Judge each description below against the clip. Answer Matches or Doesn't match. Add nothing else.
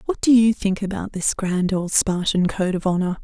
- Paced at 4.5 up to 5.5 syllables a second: Matches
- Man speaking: Doesn't match